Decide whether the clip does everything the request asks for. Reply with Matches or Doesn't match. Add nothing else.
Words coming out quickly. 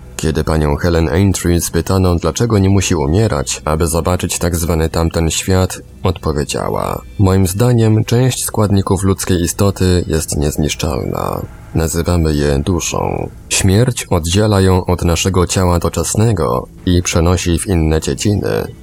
Doesn't match